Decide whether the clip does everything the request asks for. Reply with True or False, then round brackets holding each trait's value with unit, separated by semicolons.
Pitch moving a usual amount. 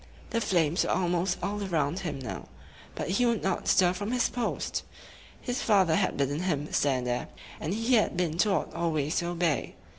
True (4.6 semitones)